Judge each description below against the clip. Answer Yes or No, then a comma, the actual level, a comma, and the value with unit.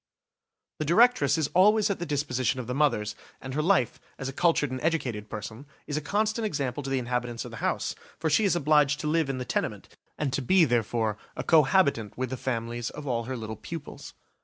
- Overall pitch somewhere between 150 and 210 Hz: No, medium, 140 Hz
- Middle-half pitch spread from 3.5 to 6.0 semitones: Yes, average, 4.7 semitones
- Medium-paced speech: No, fast, 220 wpm